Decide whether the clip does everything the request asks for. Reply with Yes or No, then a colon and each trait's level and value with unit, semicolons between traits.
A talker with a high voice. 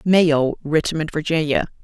No: medium, 155 Hz